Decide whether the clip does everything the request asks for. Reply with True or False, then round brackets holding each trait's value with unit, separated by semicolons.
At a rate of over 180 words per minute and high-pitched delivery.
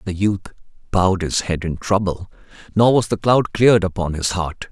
False (205 wpm; 95 Hz)